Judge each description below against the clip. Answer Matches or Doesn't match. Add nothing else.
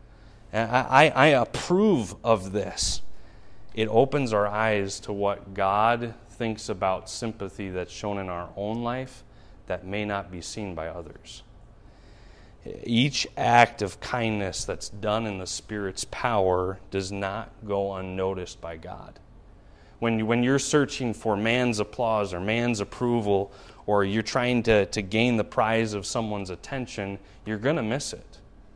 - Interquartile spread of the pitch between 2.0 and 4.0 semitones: Matches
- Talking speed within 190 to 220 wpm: Doesn't match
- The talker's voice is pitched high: Doesn't match